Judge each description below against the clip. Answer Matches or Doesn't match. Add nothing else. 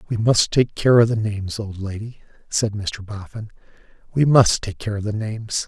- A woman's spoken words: Doesn't match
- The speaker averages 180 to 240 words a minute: Matches